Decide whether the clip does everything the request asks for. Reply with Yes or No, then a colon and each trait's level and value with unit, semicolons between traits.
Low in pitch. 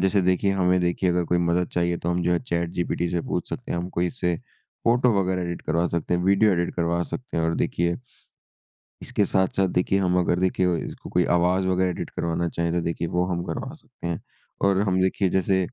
Yes: very low, 90 Hz